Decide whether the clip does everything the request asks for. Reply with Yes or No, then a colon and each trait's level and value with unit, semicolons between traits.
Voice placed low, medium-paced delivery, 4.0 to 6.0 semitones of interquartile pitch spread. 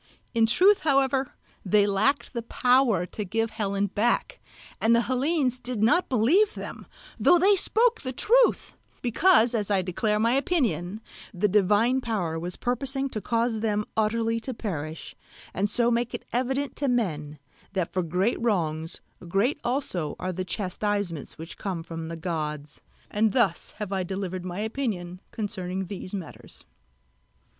No: high, 215 Hz; average, 155 wpm; average, 5.2 semitones